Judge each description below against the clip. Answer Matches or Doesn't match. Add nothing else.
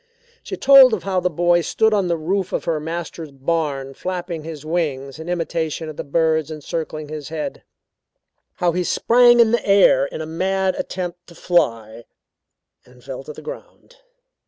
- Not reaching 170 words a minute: Doesn't match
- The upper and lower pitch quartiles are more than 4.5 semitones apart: Doesn't match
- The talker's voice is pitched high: Doesn't match